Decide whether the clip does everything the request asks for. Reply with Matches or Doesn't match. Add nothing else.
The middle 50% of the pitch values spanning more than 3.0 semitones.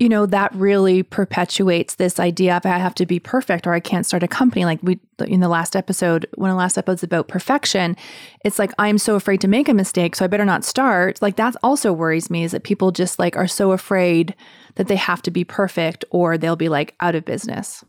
Doesn't match